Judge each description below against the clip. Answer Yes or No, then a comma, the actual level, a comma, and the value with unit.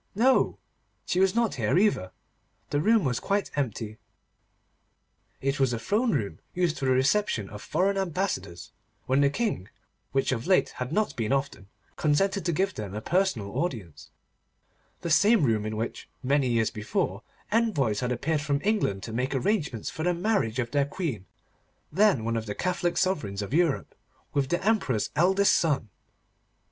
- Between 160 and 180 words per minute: Yes, average, 170 wpm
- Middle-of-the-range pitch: Yes, medium, 145 Hz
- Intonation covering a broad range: Yes, wide, 8.8 semitones